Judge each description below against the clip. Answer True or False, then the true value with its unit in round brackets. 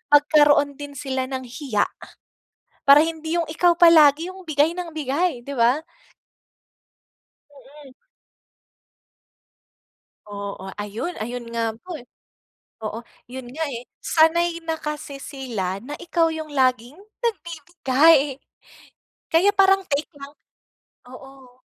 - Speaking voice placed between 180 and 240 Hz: False (285 Hz)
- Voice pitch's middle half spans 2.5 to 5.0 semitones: True (4.2 semitones)